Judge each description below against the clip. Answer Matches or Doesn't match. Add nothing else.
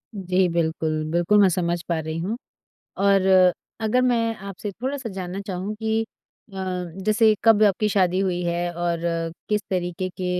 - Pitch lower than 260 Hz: Matches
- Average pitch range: Matches